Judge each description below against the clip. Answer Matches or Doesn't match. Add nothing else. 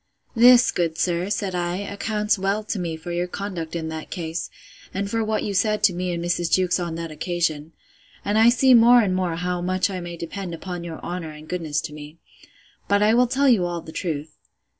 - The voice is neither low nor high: Matches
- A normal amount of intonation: Matches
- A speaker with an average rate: Doesn't match